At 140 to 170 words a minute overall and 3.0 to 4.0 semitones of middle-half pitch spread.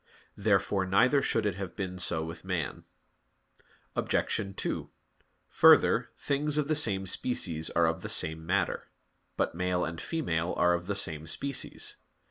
No: average, 150 wpm; average, 4.4 semitones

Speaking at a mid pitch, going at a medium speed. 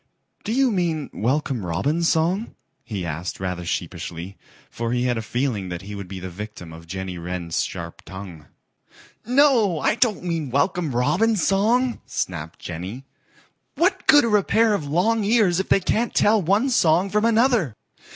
Yes: medium, 150 Hz; average, 170 wpm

